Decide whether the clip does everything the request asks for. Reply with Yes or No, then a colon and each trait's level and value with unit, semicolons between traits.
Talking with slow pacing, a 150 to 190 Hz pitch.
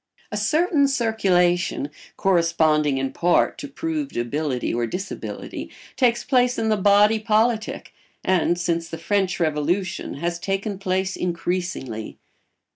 Yes: slow, 120 wpm; medium, 185 Hz